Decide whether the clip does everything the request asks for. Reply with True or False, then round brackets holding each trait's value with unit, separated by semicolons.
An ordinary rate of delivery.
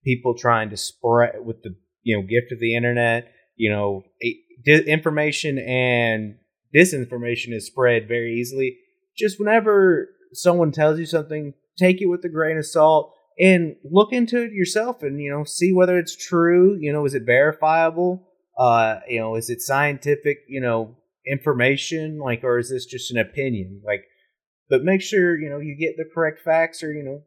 True (180 wpm)